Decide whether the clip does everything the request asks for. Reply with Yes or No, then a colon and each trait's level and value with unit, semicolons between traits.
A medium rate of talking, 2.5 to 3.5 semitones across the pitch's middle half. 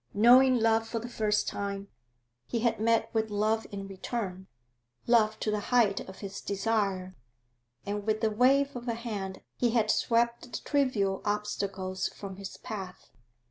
Yes: average, 160 wpm; average, 2.8 semitones